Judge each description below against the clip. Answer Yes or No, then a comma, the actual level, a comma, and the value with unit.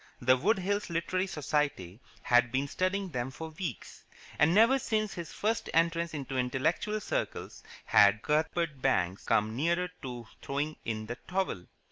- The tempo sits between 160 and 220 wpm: No, average, 150 wpm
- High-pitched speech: No, medium, 155 Hz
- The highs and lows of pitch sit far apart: Yes, wide, 6.7 semitones